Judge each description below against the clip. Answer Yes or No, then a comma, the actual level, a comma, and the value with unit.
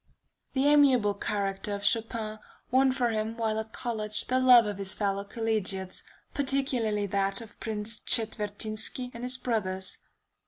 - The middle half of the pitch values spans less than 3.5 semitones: Yes, average, 3.1 semitones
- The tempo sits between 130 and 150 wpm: Yes, average, 145 wpm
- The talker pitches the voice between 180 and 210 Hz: No, high, 220 Hz